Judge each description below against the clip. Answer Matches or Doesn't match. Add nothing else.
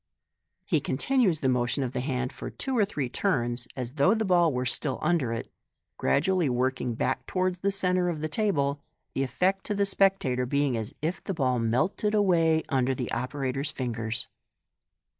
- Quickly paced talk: Doesn't match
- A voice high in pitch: Doesn't match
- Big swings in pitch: Matches